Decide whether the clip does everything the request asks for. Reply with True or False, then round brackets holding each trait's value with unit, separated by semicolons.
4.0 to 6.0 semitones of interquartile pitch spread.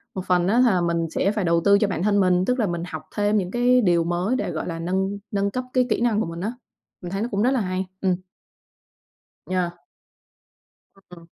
False (3.3 semitones)